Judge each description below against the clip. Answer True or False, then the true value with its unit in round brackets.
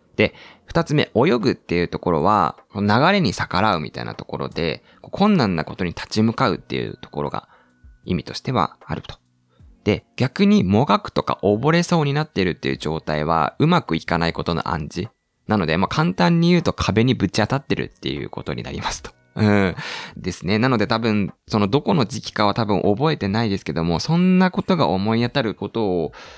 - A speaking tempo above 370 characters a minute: True (380 characters per minute)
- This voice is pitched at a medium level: False (105 Hz)